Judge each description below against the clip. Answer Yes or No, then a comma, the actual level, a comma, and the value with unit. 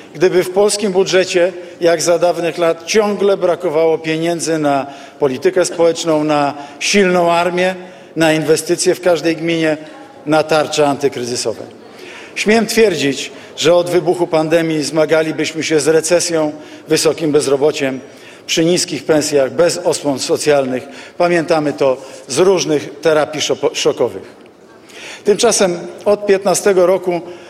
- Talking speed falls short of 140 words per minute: Yes, average, 115 wpm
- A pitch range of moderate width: Yes, average, 3.0 semitones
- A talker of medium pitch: Yes, medium, 165 Hz